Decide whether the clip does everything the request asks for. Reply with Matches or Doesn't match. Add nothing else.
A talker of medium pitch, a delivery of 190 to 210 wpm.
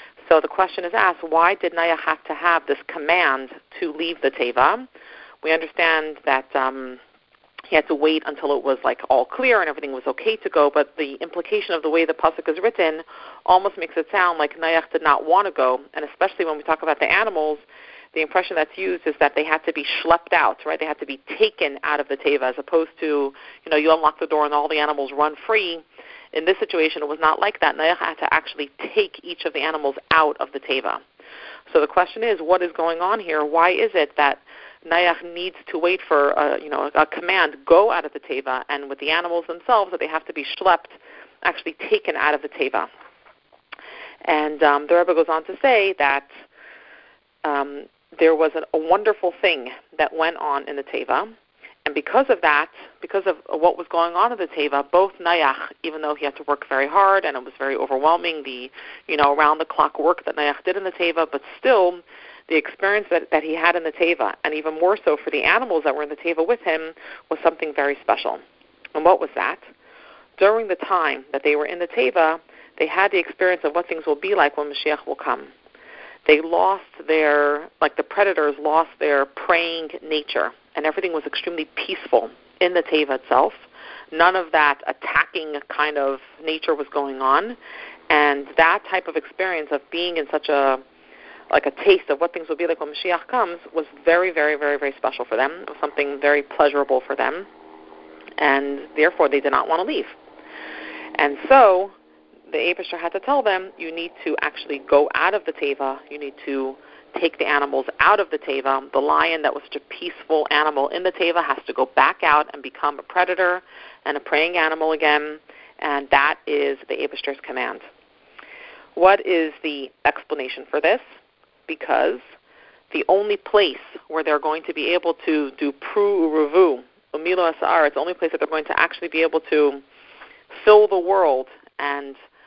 Matches